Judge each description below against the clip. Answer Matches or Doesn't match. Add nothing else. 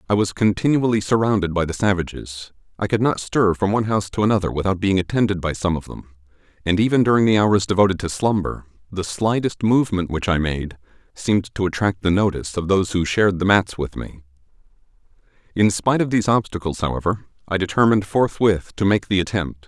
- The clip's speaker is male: Matches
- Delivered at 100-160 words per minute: Doesn't match